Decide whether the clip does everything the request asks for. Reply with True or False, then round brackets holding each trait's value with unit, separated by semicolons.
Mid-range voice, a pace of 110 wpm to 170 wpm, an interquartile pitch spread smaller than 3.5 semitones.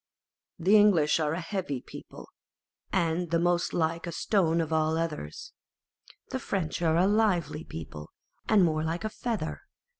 True (170 Hz; 155 wpm; 3.1 semitones)